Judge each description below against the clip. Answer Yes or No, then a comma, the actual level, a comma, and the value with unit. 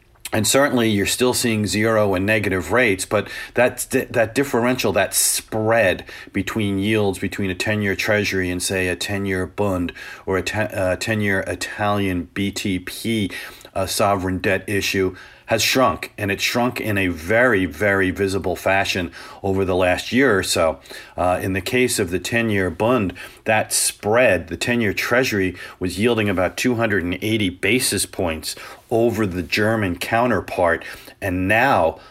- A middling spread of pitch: Yes, average, 3.3 semitones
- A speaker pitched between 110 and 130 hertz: No, low, 100 Hz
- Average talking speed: Yes, average, 155 wpm